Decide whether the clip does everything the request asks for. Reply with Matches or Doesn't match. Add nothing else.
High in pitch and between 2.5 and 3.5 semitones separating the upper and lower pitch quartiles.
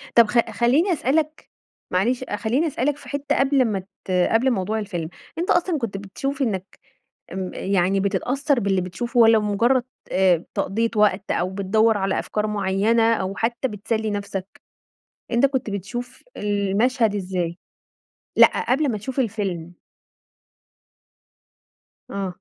Doesn't match